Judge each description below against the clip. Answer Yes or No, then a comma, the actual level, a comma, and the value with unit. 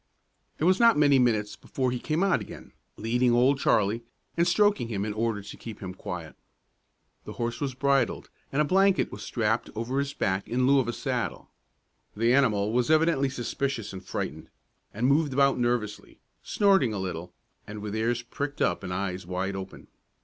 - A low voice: Yes, low, 120 Hz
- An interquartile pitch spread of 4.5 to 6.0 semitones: Yes, average, 5.1 semitones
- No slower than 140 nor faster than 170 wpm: No, average, 185 wpm